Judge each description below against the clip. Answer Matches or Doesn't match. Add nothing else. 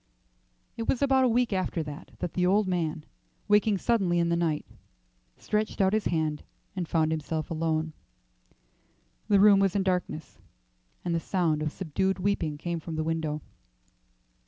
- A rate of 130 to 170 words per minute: Matches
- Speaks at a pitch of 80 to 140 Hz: Doesn't match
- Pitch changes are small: Doesn't match